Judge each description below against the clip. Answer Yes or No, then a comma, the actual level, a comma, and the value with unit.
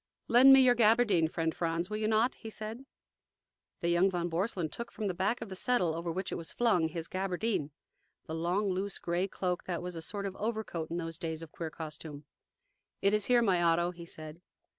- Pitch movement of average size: Yes, average, 4.3 semitones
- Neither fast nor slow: No, fast, 215 wpm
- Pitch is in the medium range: Yes, medium, 180 Hz